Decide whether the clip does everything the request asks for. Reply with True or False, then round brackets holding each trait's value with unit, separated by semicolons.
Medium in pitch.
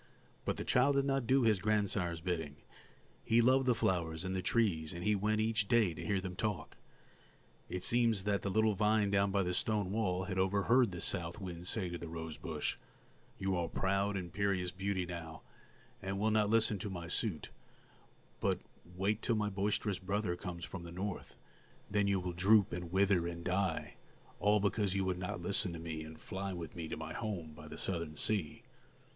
False (95 Hz)